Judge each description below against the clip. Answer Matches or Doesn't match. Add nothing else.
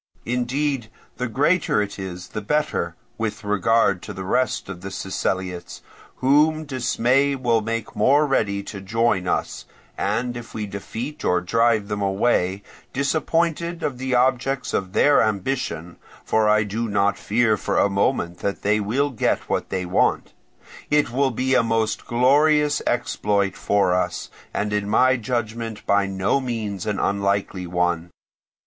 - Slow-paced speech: Doesn't match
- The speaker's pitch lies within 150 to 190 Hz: Doesn't match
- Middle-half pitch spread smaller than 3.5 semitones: Doesn't match